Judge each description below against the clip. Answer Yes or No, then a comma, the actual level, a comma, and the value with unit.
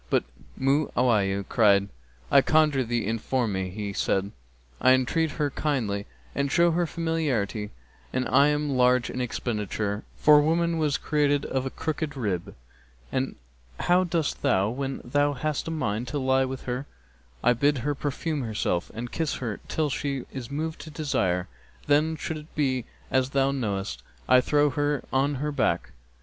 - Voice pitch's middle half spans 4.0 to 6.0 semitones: Yes, average, 4.3 semitones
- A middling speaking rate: Yes, average, 160 wpm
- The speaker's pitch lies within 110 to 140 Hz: Yes, low, 135 Hz